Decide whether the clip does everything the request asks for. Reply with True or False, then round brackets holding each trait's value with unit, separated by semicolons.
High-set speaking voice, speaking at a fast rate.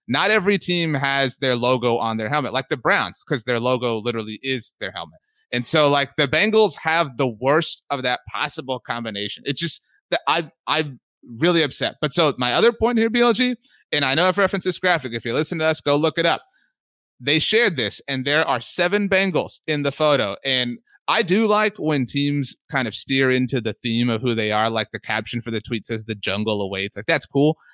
False (140 Hz; 220 wpm)